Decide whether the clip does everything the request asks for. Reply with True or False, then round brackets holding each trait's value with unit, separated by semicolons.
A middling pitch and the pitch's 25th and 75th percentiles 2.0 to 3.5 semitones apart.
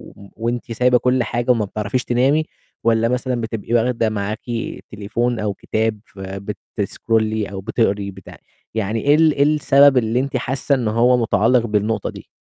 False (115 Hz; 3.0 semitones)